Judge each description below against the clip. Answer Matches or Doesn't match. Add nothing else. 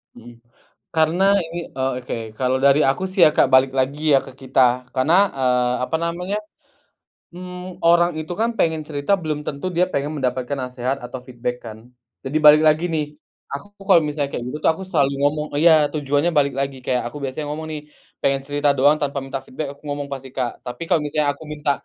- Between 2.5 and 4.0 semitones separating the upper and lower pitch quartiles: Matches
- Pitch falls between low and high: Matches